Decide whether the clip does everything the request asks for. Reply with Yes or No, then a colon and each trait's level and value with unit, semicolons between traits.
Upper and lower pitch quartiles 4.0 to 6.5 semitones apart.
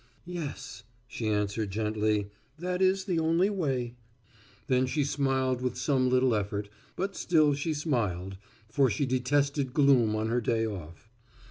Yes: average, 5.1 semitones